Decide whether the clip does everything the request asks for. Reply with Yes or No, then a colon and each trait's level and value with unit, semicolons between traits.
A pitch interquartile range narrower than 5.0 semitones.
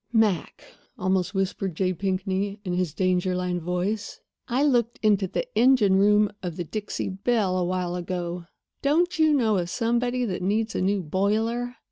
Yes: average, 3.8 semitones